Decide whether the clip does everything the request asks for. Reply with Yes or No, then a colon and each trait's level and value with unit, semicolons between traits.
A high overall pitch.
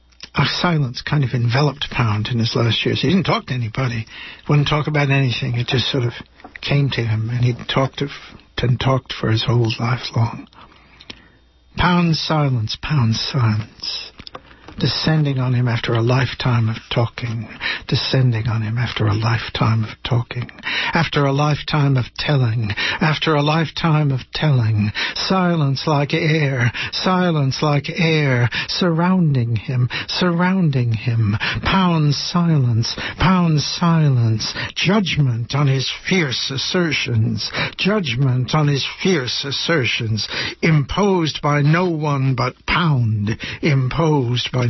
No: low, 135 Hz